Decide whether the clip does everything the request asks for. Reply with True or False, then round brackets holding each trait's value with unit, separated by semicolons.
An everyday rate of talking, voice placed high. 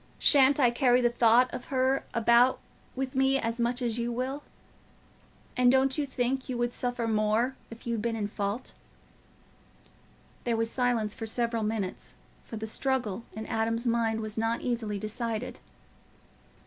True (160 wpm; 235 Hz)